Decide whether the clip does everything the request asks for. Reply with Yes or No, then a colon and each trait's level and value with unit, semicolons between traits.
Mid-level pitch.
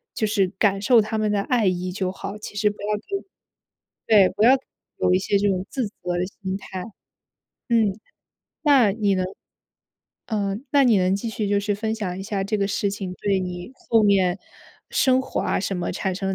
No: high, 200 Hz